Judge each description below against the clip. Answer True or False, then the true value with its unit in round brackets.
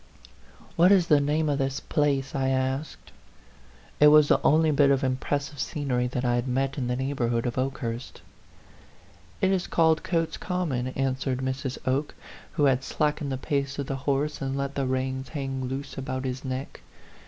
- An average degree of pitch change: False (2.1 semitones)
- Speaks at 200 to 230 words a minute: False (190 wpm)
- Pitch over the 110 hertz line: True (135 Hz)